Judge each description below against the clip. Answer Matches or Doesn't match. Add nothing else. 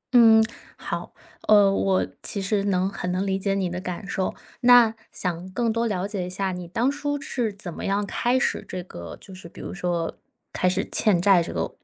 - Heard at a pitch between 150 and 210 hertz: Matches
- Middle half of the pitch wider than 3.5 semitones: Doesn't match